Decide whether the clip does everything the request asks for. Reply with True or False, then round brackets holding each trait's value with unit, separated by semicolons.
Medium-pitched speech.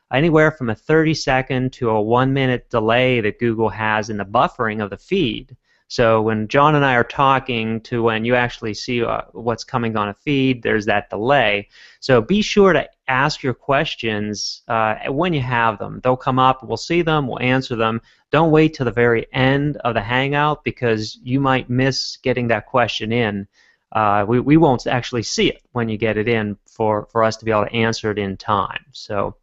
False (120 Hz)